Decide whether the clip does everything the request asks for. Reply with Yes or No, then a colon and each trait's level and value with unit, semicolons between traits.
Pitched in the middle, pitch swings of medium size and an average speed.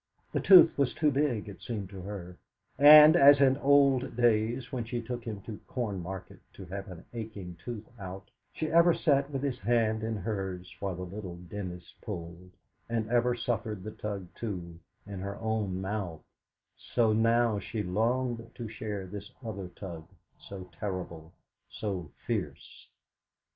No: low, 105 Hz; average, 4.2 semitones; average, 160 wpm